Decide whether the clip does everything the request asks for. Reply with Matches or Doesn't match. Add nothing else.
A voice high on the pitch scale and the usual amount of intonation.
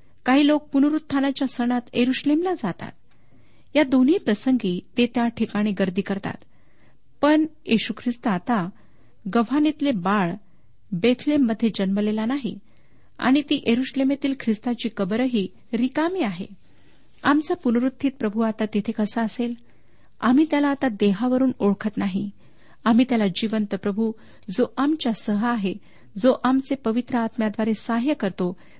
Matches